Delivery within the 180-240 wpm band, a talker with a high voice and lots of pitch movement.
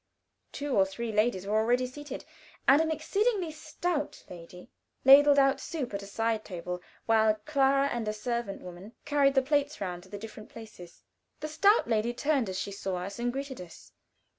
Yes: average, 185 wpm; high, 235 Hz; wide, 6.1 semitones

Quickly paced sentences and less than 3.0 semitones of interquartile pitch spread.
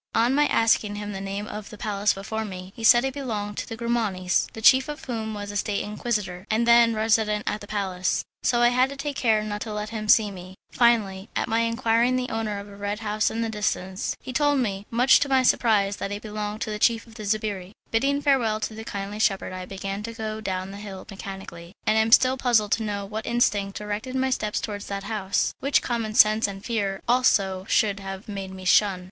Yes: fast, 235 wpm; narrow, 2.5 semitones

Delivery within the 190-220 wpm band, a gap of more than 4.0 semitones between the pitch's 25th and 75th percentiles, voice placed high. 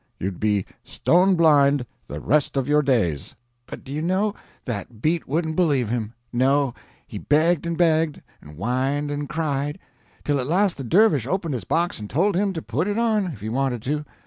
No: average, 195 wpm; average, 5.2 semitones; medium, 145 Hz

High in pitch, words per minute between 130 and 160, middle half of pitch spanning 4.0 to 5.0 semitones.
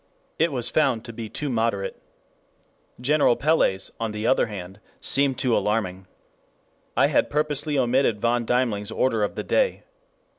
No: low, 120 Hz; average, 150 wpm; average, 4.7 semitones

